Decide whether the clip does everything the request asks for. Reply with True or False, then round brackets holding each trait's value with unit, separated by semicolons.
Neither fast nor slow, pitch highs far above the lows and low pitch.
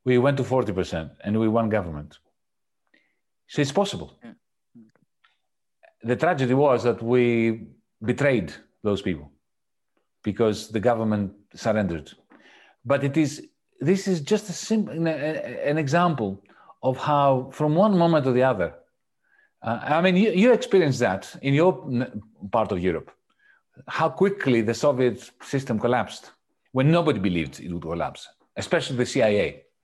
True (135 wpm; 6.7 semitones; 130 Hz)